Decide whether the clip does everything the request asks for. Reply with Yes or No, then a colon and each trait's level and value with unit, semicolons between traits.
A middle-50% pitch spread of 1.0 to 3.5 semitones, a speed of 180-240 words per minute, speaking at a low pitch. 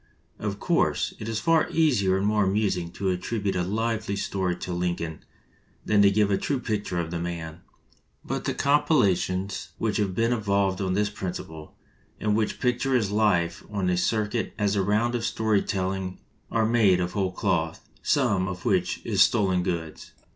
Yes: average, 3.1 semitones; average, 190 wpm; low, 100 Hz